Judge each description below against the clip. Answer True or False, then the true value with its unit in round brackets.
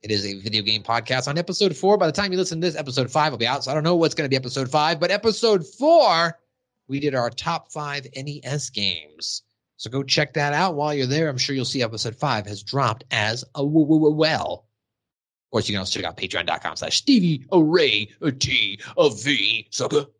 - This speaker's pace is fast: True (215 wpm)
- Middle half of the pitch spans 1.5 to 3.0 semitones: False (5.1 semitones)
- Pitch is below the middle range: False (145 Hz)